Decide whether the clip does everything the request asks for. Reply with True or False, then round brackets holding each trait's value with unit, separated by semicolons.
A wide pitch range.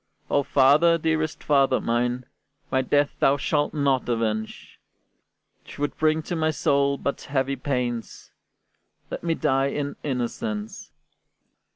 False (2.8 semitones)